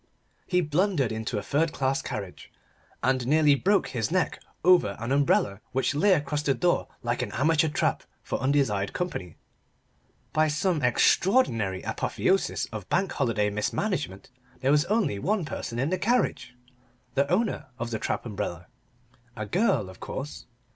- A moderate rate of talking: Yes, average, 155 wpm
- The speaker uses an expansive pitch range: Yes, wide, 8.2 semitones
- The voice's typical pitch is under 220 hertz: Yes, medium, 140 Hz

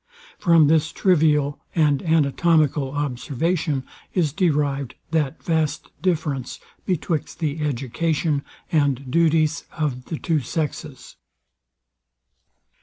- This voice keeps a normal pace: No, slow, 95 wpm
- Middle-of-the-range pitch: Yes, medium, 150 Hz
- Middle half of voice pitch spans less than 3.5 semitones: Yes, narrow, 2.6 semitones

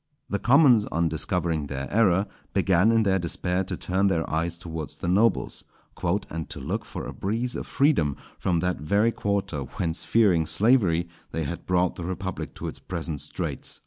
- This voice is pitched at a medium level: No, very low, 90 Hz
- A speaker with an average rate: Yes, average, 175 wpm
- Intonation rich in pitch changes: No, average, 3.8 semitones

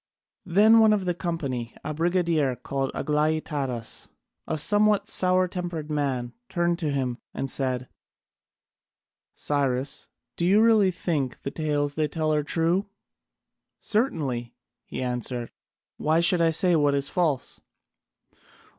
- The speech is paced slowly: Yes, slow, 130 wpm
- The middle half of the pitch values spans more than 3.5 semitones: Yes, average, 4.6 semitones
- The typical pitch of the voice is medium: Yes, medium, 155 Hz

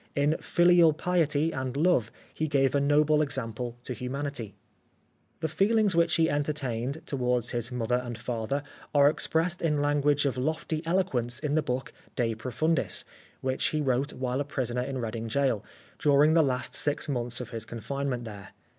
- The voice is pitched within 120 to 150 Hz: Yes, medium, 140 Hz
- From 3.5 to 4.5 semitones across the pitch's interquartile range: Yes, average, 3.8 semitones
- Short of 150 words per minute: No, average, 170 wpm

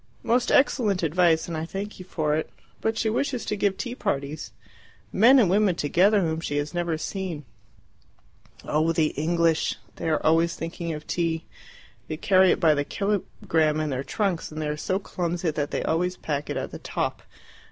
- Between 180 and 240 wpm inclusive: Yes, average, 190 wpm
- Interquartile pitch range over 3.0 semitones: Yes, average, 3.9 semitones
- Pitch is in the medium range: Yes, medium, 170 Hz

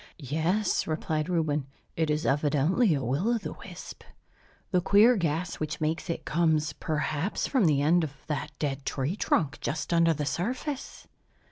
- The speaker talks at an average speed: Yes, average, 160 wpm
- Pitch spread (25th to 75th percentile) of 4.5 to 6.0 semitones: No, average, 3.3 semitones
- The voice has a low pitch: No, medium, 155 Hz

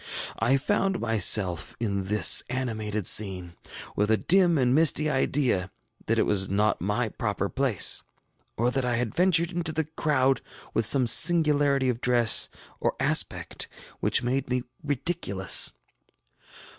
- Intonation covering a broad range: Yes, wide, 5.7 semitones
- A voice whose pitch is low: Yes, low, 125 Hz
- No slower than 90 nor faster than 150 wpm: Yes, average, 140 wpm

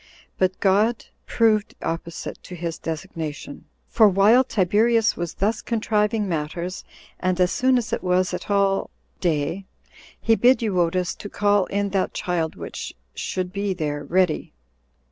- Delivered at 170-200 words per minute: No, average, 145 wpm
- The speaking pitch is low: No, high, 190 Hz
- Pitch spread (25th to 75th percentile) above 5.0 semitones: No, average, 3.3 semitones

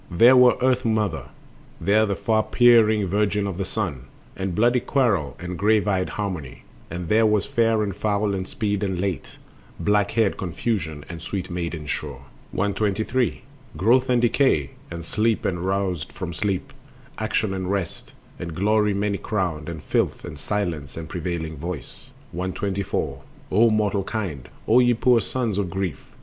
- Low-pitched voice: Yes, low, 100 Hz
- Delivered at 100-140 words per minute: No, average, 160 wpm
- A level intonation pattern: No, average, 3.7 semitones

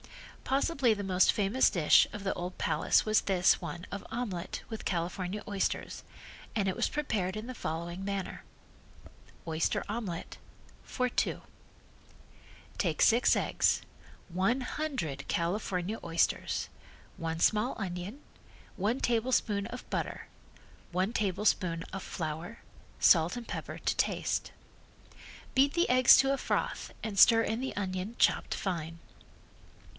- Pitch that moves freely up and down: No, average, 4.7 semitones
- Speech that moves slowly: Yes, slow, 130 wpm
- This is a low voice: No, high, 200 Hz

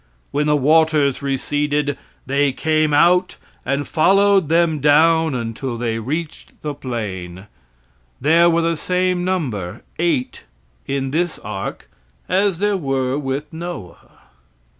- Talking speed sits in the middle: No, slow, 120 wpm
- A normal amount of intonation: Yes, average, 4.0 semitones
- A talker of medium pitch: Yes, medium, 150 Hz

